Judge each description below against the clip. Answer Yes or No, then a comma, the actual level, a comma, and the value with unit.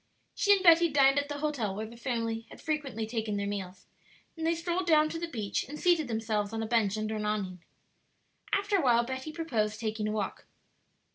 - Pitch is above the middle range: Yes, high, 235 Hz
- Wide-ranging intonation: Yes, wide, 6.3 semitones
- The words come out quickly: Yes, fast, 210 wpm